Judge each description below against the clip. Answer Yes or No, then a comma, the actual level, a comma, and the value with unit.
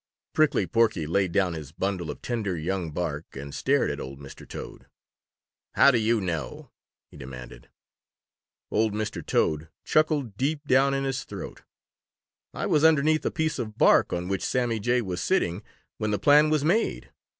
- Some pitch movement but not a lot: No, wide, 8.3 semitones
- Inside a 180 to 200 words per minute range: No, average, 170 wpm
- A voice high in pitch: No, low, 105 Hz